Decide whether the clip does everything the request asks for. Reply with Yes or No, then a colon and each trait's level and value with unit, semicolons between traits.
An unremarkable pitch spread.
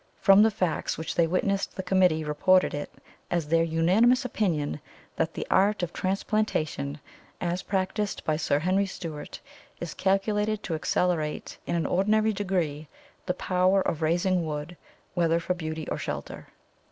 Yes: average, 3.5 semitones